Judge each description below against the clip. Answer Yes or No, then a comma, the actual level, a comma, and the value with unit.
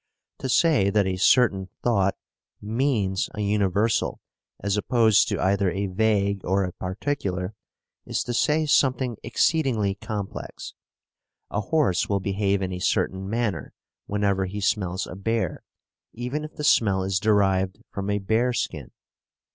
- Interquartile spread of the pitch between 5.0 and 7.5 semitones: No, average, 3.2 semitones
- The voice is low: Yes, low, 100 Hz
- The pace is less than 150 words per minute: Yes, average, 140 wpm